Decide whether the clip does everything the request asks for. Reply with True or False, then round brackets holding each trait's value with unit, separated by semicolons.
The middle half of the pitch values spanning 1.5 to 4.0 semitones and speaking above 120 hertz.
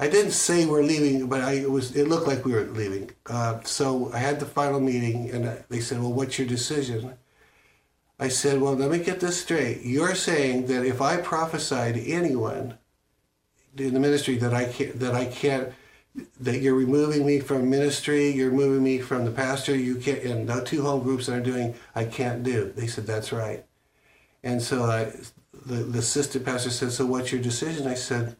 True (2.5 semitones; 130 Hz)